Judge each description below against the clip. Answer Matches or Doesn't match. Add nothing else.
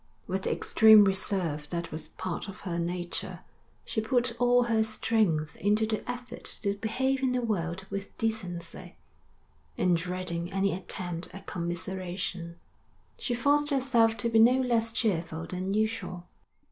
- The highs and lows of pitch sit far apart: Doesn't match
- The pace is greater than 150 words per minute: Doesn't match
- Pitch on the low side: Doesn't match